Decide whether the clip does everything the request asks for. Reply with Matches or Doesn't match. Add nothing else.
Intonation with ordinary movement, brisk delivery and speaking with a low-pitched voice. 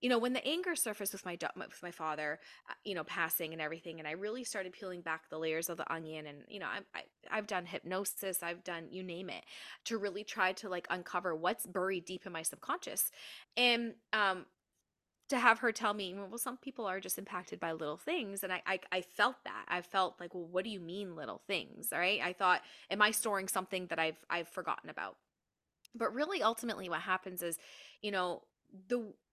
Doesn't match